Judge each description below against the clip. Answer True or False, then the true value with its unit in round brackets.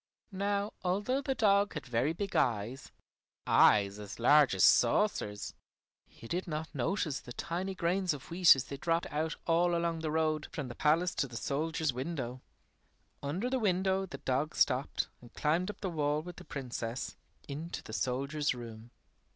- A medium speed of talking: True (170 wpm)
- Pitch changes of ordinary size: False (5.7 semitones)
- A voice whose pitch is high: False (155 Hz)